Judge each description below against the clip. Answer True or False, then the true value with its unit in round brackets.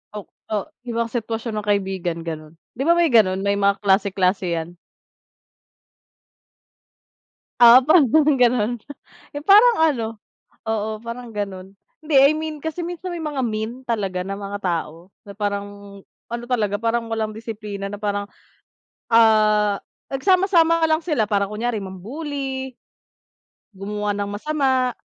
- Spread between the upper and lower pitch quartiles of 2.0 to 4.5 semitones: False (4.9 semitones)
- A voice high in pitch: True (220 Hz)